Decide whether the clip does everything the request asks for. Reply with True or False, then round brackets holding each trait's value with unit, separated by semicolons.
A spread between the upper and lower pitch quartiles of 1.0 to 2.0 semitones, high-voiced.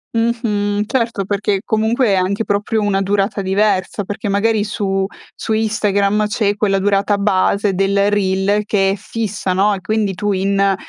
True (1.5 semitones; 205 Hz)